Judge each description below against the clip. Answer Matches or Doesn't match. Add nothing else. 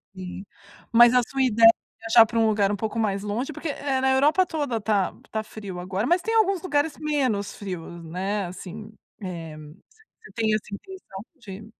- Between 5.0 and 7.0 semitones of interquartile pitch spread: Matches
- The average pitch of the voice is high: Matches